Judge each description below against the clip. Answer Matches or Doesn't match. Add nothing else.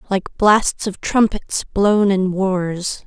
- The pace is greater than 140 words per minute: Doesn't match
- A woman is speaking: Matches